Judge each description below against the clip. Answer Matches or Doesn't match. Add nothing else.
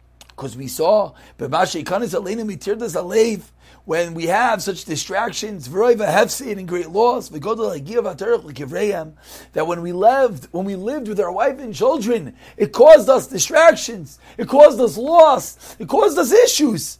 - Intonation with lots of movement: Matches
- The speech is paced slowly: Matches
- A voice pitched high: Matches